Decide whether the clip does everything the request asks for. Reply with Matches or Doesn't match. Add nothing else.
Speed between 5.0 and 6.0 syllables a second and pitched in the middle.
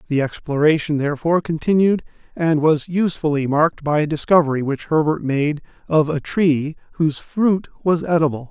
Matches